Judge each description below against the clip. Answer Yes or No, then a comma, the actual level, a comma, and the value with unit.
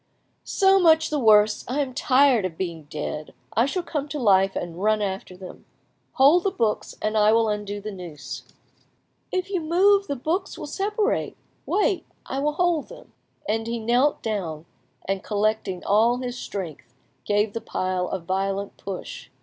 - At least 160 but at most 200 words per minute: Yes, average, 170 wpm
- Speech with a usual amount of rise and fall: No, wide, 7.3 semitones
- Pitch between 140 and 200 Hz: No, high, 220 Hz